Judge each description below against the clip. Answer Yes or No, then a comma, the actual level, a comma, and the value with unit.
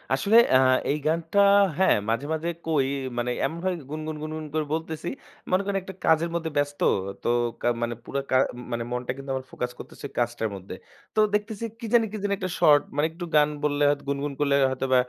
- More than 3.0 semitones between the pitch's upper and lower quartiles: Yes, average, 4.1 semitones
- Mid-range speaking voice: Yes, medium, 150 Hz